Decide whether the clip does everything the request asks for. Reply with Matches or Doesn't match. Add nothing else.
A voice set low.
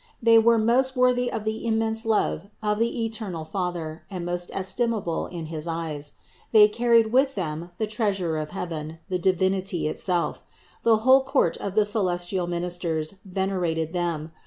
Doesn't match